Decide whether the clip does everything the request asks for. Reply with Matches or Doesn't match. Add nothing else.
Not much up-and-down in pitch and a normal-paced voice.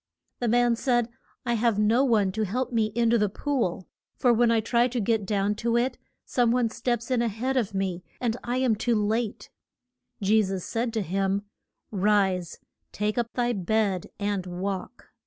Doesn't match